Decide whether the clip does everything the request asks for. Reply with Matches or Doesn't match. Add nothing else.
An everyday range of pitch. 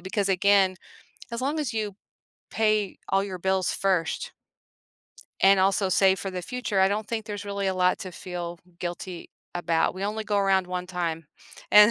Doesn't match